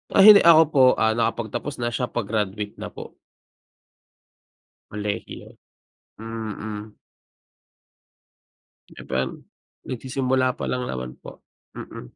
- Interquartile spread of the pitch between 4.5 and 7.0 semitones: No, average, 3.7 semitones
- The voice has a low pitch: Yes, low, 115 Hz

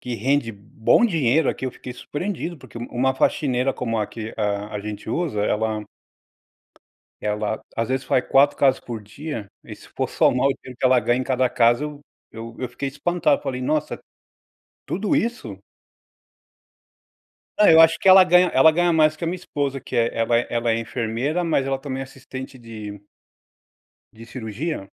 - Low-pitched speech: Yes, low, 130 Hz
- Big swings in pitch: No, average, 4.6 semitones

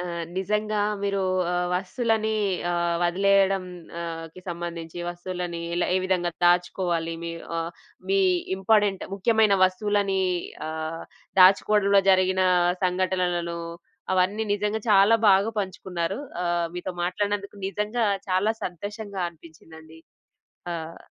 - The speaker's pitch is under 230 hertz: Yes, medium, 185 Hz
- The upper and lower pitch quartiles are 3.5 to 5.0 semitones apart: No, average, 2.7 semitones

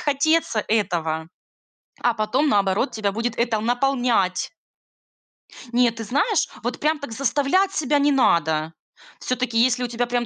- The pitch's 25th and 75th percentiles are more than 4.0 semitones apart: Yes, average, 4.5 semitones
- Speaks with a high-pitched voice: Yes, high, 240 Hz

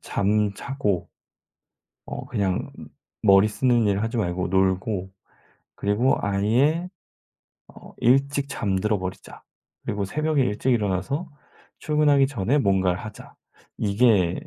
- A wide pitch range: Yes, wide, 5.7 semitones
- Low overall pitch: Yes, low, 105 Hz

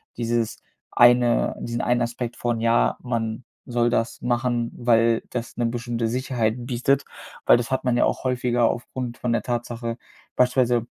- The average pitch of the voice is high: No, low, 120 Hz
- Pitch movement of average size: No, narrow, 0.9 semitones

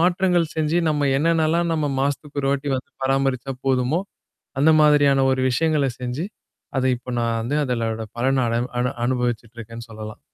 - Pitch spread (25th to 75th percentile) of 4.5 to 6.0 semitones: No, average, 3.7 semitones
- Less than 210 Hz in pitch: Yes, low, 135 Hz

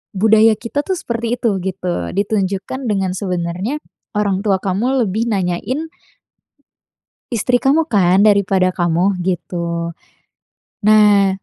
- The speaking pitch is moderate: No, high, 200 Hz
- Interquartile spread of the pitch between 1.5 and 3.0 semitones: No, average, 3.5 semitones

